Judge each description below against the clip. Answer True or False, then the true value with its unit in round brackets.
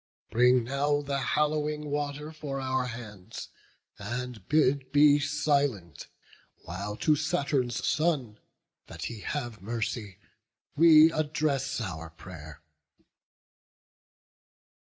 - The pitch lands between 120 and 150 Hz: True (135 Hz)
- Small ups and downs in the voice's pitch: False (4.9 semitones)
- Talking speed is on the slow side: True (95 wpm)